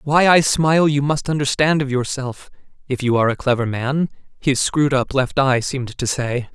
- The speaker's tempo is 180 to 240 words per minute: Yes, average, 200 wpm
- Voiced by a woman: No, male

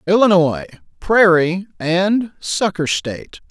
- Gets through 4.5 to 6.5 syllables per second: No, 3.7 syllables/s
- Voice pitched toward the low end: No, medium, 185 Hz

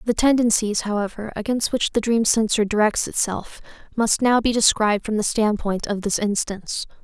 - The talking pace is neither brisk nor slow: Yes, average, 170 wpm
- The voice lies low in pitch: No, high, 215 Hz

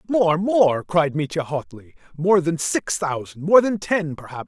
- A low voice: No, medium, 165 Hz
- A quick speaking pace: No, average, 175 wpm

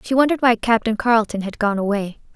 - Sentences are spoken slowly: No, fast, 205 wpm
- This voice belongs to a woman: Yes, female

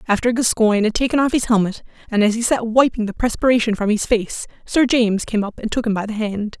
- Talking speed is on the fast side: Yes, fast, 245 wpm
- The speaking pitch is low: No, high, 225 Hz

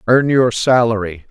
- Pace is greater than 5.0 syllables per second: No, 4.4 syllables/s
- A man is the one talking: Yes, male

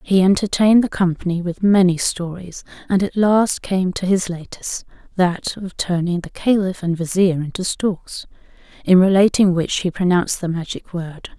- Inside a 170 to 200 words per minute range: No, average, 155 wpm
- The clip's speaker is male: No, female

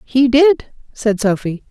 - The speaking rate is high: No, average, 140 wpm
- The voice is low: No, high, 245 Hz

